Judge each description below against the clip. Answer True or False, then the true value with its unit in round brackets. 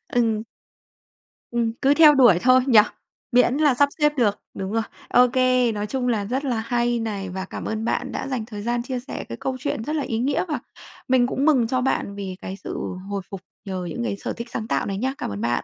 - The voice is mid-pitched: False (240 Hz)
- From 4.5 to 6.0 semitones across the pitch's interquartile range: False (3.8 semitones)